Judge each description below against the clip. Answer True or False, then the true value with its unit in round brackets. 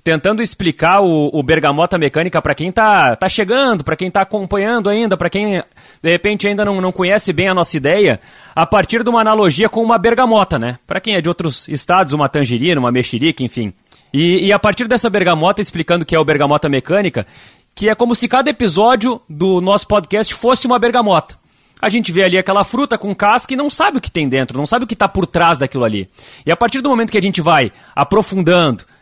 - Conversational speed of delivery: False (220 wpm)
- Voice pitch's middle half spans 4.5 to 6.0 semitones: True (5.4 semitones)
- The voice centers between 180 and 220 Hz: True (190 Hz)